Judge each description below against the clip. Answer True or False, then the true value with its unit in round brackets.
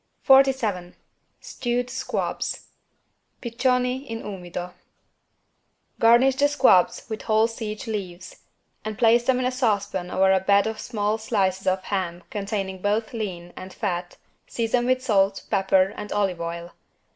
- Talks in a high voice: True (210 Hz)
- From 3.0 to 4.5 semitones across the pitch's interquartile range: True (4.1 semitones)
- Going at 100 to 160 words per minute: True (135 wpm)